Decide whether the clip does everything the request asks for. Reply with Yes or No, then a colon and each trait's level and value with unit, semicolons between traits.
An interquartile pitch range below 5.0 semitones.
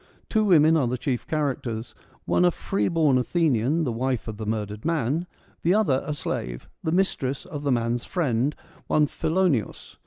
No: wide, 5.6 semitones